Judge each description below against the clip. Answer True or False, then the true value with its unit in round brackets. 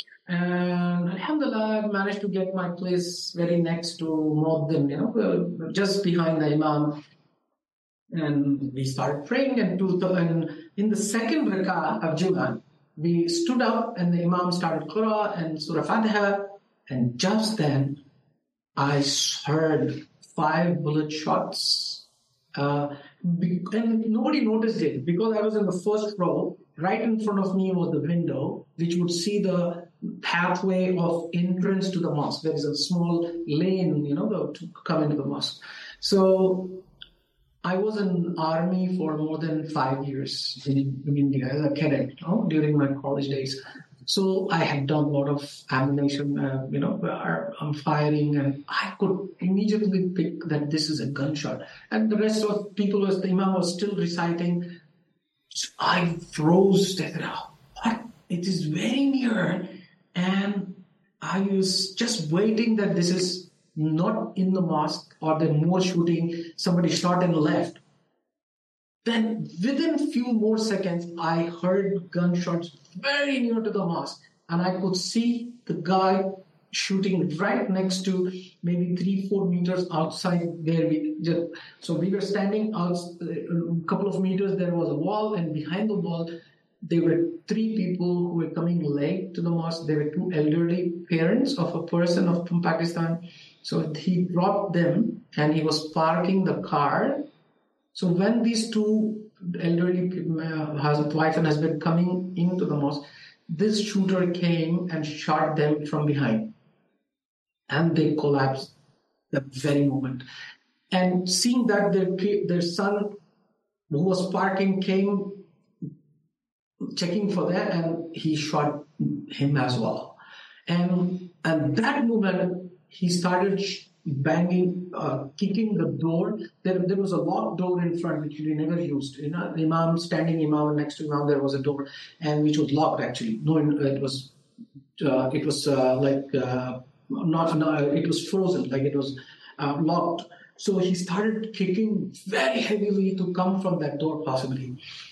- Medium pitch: True (175 Hz)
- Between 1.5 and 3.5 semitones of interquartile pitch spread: False (3.9 semitones)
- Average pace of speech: False (155 wpm)